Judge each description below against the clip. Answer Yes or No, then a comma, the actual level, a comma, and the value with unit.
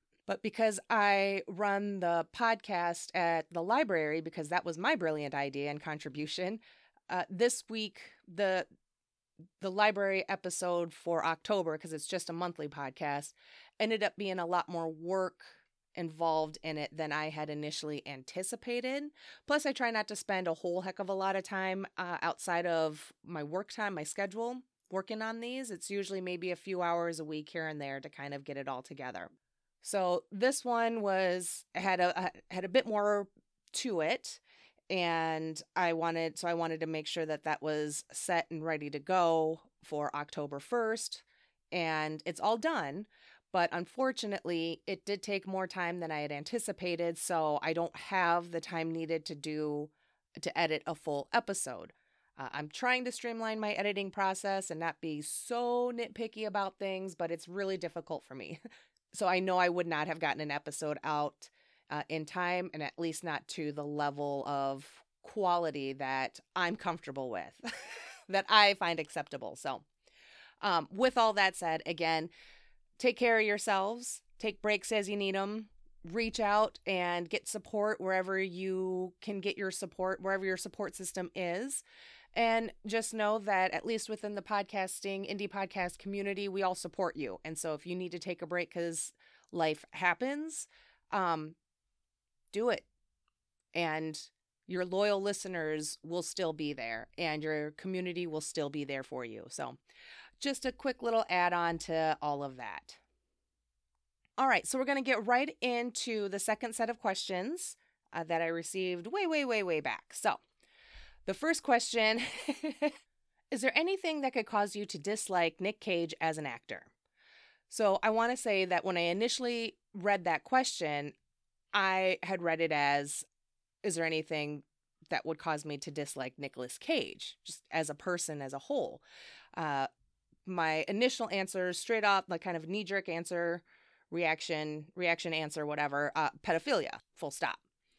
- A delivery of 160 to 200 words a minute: Yes, average, 170 wpm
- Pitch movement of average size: Yes, average, 4.4 semitones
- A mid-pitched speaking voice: Yes, medium, 180 Hz